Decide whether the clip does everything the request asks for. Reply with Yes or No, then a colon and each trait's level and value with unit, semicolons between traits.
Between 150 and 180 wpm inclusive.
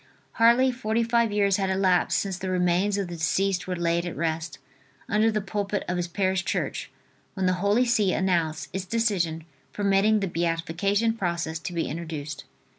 Yes: average, 175 wpm